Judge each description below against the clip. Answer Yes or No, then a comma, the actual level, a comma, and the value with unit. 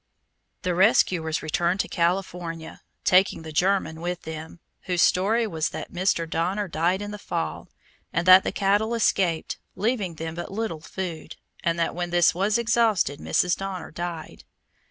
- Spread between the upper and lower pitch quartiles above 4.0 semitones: No, average, 2.9 semitones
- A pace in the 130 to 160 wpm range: Yes, average, 155 wpm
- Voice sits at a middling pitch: Yes, medium, 180 Hz